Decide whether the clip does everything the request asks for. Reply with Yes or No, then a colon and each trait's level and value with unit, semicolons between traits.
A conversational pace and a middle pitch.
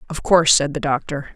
No: fast, 220 wpm; medium, 150 Hz